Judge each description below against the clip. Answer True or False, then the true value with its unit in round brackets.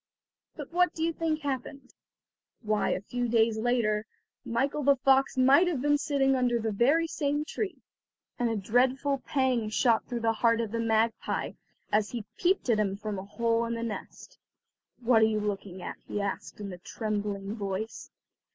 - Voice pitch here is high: True (230 Hz)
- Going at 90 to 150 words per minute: False (185 wpm)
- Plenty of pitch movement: False (4.1 semitones)